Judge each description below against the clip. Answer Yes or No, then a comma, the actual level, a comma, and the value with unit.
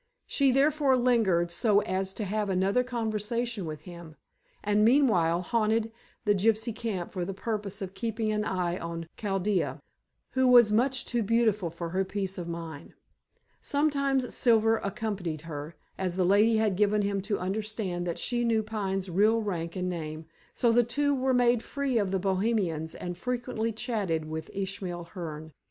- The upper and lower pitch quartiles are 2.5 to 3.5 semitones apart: No, average, 4.4 semitones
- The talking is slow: No, average, 165 wpm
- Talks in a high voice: Yes, high, 205 Hz